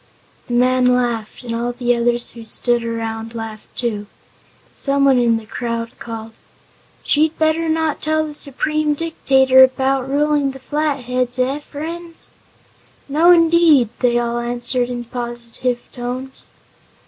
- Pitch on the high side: Yes, very high, 250 Hz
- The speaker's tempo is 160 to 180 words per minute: No, slow, 135 wpm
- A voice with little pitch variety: No, average, 3.6 semitones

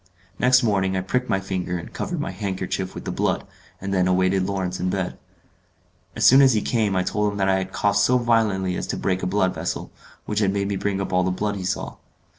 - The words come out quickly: Yes, fast, 240 wpm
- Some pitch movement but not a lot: No, narrow, 2.0 semitones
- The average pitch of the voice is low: Yes, very low, 95 Hz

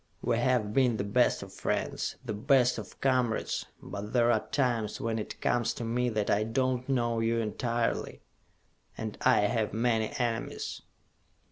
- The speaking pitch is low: Yes, low, 115 Hz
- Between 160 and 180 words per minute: Yes, average, 165 wpm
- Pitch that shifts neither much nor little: No, narrow, 2.2 semitones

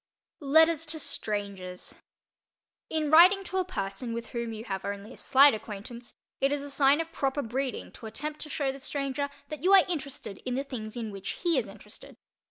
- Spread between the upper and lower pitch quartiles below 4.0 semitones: No, wide, 5.5 semitones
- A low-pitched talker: No, very high, 270 Hz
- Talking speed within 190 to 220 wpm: Yes, average, 195 wpm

